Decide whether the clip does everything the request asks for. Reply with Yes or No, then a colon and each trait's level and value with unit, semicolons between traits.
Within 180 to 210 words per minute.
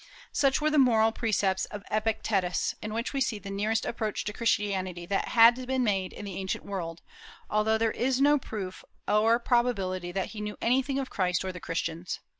Yes: average, 195 wpm